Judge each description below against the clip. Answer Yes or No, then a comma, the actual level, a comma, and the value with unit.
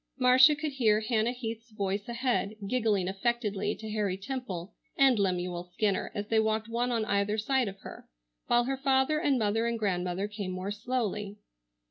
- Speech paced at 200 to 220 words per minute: No, average, 170 wpm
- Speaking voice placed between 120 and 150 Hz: No, high, 220 Hz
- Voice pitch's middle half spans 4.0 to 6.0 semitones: No, average, 3.5 semitones